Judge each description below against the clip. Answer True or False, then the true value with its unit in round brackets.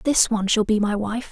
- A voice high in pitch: True (220 Hz)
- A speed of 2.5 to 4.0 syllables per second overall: False (5.9 syllables/s)